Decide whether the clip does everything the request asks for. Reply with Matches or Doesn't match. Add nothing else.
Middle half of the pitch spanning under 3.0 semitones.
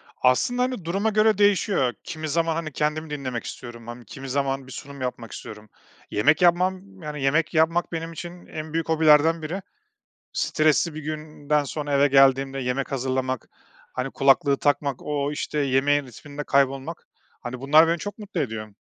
Doesn't match